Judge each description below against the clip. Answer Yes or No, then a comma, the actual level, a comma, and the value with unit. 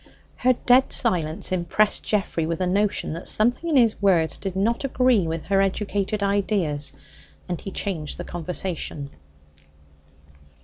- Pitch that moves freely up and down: No, average, 4.1 semitones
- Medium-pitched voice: No, high, 195 Hz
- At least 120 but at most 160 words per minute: Yes, average, 140 wpm